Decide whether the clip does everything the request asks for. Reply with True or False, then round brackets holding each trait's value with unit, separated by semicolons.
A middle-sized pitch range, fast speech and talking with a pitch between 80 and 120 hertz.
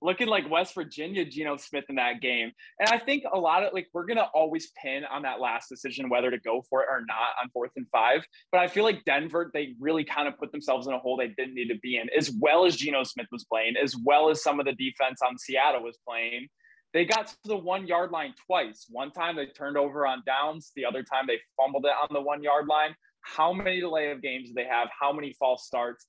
False (4.1 semitones; 260 wpm; 140 Hz)